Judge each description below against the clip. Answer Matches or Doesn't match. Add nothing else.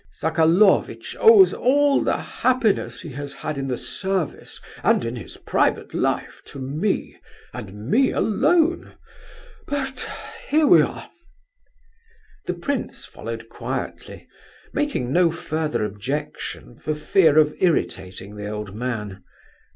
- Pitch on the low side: Doesn't match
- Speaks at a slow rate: Matches